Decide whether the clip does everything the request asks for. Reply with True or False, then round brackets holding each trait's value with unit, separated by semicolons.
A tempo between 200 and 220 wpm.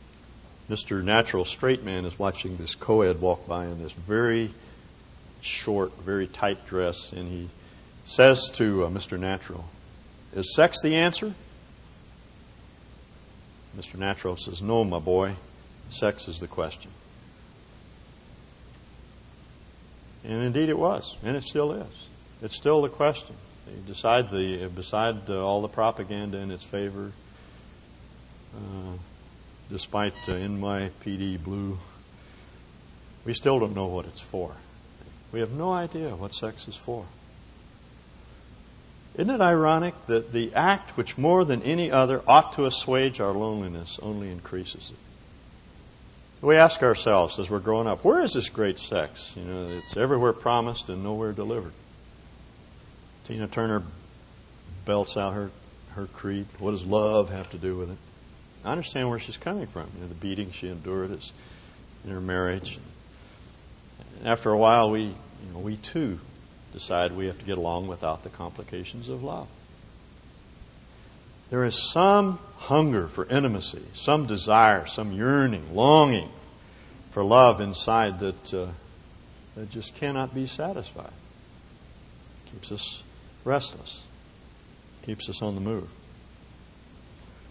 False (140 wpm)